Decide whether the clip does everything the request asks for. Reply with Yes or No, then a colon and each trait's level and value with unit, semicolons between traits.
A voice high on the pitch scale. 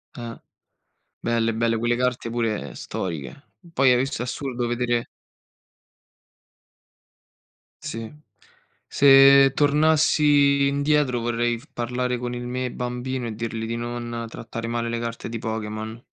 No: low, 120 Hz